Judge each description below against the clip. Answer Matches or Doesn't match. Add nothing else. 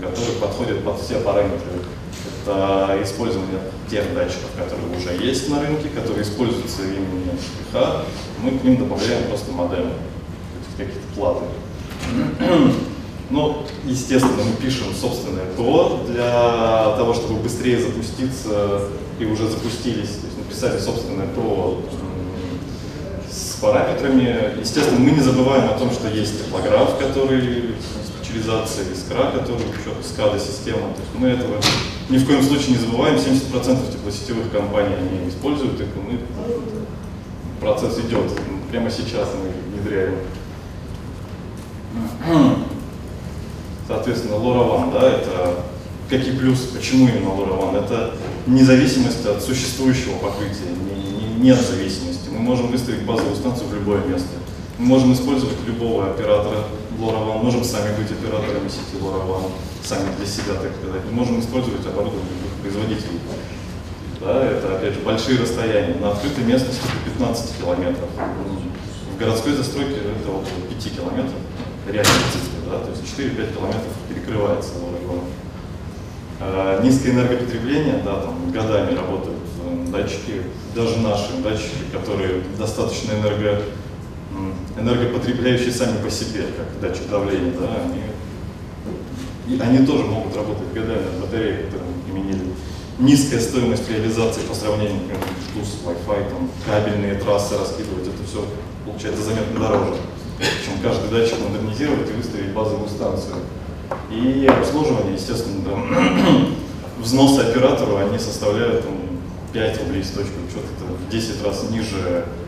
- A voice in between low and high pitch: Doesn't match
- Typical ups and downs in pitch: Matches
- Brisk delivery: Doesn't match